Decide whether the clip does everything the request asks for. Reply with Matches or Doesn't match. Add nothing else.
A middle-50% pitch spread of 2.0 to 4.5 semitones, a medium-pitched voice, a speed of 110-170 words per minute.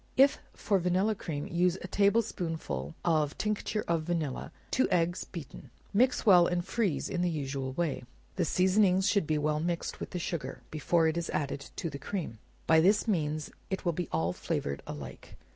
Doesn't match